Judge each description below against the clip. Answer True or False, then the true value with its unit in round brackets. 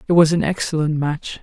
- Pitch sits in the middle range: True (160 Hz)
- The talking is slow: False (210 wpm)